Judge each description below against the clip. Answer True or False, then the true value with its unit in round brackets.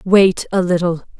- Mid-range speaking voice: True (180 Hz)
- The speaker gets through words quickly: False (150 wpm)